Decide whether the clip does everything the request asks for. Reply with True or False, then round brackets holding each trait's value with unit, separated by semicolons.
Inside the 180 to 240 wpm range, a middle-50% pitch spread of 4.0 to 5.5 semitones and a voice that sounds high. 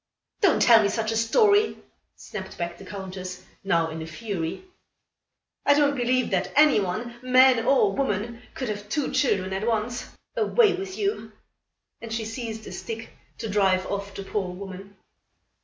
False (165 wpm; 4.7 semitones; 220 Hz)